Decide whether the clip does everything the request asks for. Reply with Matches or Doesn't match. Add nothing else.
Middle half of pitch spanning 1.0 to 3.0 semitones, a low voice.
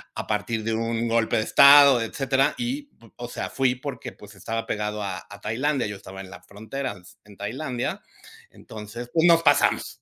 Doesn't match